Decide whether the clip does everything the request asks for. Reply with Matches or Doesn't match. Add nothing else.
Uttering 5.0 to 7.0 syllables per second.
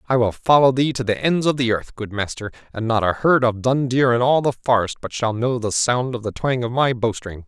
Matches